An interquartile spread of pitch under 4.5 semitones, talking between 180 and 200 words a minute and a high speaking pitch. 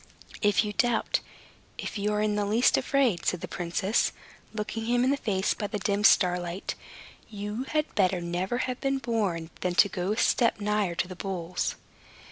Yes: average, 3.9 semitones; average, 185 wpm; high, 205 Hz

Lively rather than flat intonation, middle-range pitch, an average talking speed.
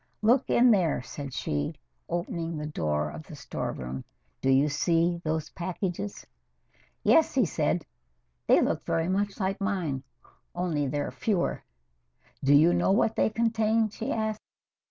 Yes: wide, 6.3 semitones; medium, 175 Hz; average, 145 wpm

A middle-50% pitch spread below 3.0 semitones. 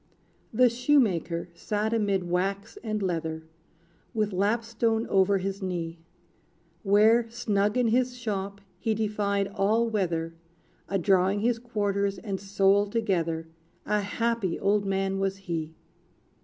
Yes: narrow, 2.6 semitones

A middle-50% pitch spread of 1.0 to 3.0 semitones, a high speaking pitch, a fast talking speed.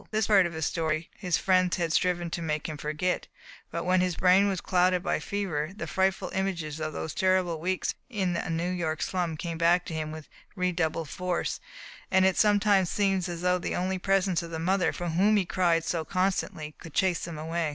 No: narrow, 2.4 semitones; medium, 180 Hz; fast, 210 wpm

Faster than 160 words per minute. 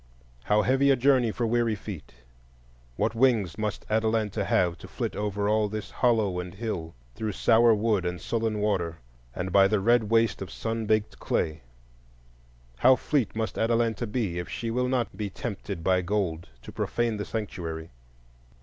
Yes: average, 170 wpm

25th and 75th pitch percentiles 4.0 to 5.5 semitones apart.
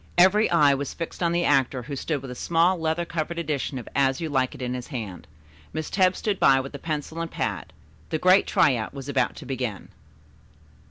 Yes: average, 4.3 semitones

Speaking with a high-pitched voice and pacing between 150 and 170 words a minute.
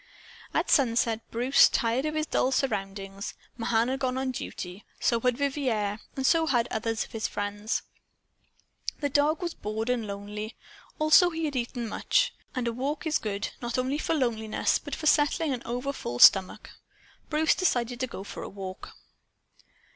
Yes: high, 245 Hz; average, 165 wpm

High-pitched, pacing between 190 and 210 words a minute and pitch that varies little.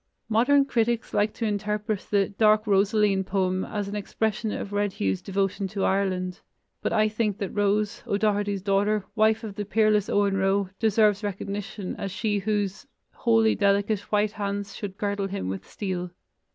No: high, 205 Hz; average, 165 wpm; narrow, 1.5 semitones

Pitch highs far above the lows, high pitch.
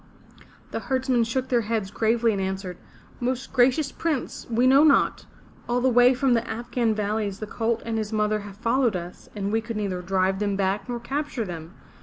No: average, 3.5 semitones; high, 225 Hz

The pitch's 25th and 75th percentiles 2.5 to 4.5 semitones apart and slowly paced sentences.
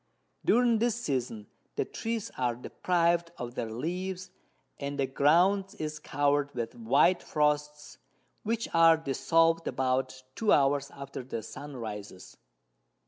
No: average, 5.0 semitones; slow, 130 wpm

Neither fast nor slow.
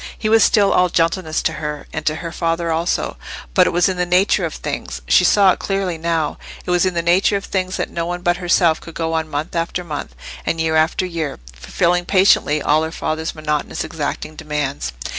No: fast, 210 wpm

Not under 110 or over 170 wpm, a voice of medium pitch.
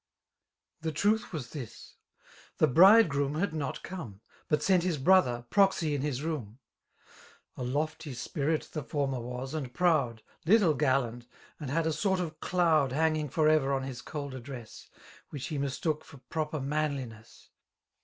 Yes: average, 160 wpm; medium, 150 Hz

